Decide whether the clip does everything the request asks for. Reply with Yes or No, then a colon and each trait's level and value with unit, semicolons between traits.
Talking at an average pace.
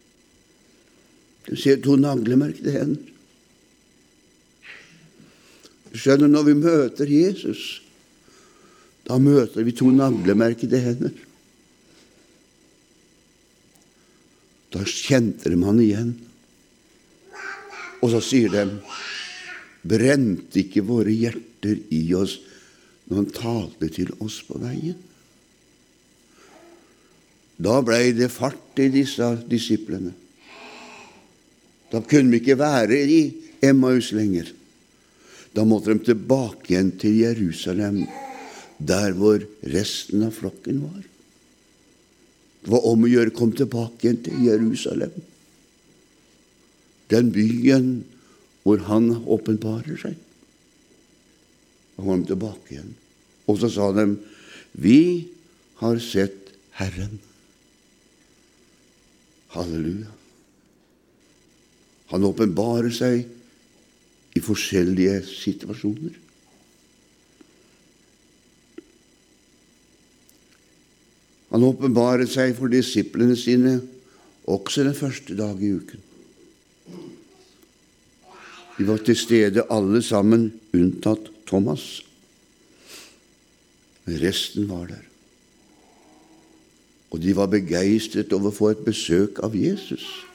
No: slow, 90 wpm